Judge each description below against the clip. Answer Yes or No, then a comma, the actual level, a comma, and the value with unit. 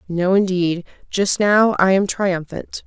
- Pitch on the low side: No, high, 190 Hz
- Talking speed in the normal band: Yes, average, 145 wpm